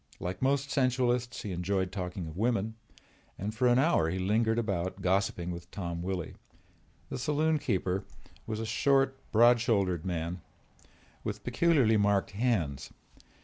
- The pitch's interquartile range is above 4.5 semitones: Yes, average, 5.2 semitones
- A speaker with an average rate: Yes, average, 145 wpm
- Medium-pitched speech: No, low, 105 Hz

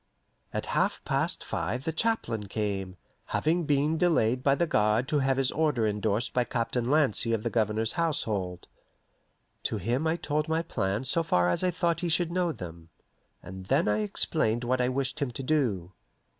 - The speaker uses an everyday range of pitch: No, wide, 6.7 semitones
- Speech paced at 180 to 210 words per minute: Yes, average, 185 wpm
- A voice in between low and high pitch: No, low, 125 Hz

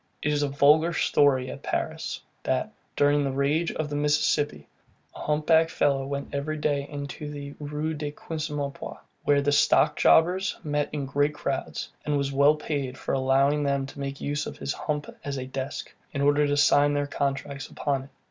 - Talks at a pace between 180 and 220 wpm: Yes, average, 190 wpm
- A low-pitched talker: No, medium, 145 Hz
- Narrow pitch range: Yes, narrow, 1.1 semitones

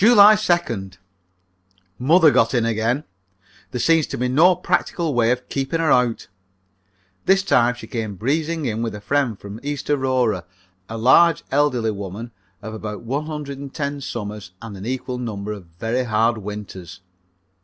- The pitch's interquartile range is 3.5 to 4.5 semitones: No, average, 5.0 semitones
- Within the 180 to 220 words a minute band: No, average, 165 wpm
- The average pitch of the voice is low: Yes, low, 125 Hz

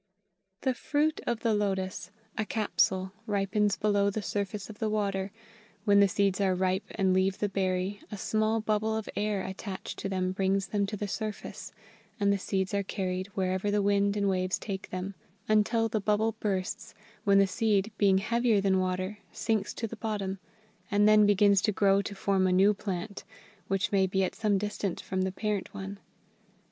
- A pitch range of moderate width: No, narrow, 1.7 semitones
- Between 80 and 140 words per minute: No, average, 190 wpm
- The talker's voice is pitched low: No, high, 200 Hz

